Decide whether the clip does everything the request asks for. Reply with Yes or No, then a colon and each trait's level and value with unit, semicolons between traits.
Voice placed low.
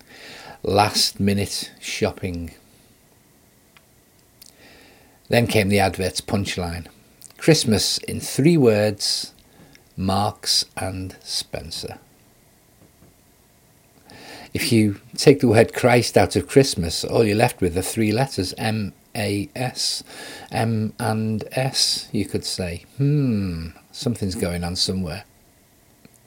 Yes: low, 105 Hz